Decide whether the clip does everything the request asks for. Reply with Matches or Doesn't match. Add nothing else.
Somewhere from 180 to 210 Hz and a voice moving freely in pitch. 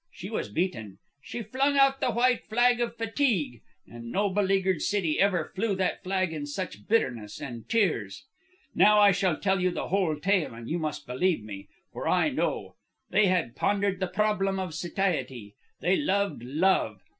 Matches